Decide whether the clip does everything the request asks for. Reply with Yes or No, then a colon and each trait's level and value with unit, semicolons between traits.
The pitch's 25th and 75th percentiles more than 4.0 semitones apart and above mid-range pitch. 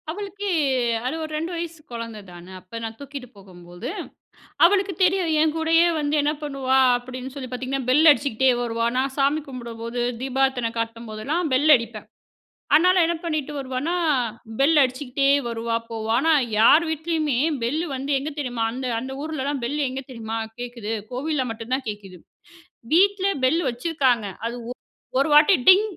Yes: average, 4.8 semitones; very high, 265 Hz